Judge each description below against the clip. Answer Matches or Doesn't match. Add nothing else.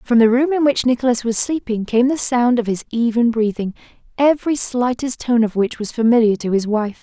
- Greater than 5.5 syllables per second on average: Doesn't match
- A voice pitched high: Matches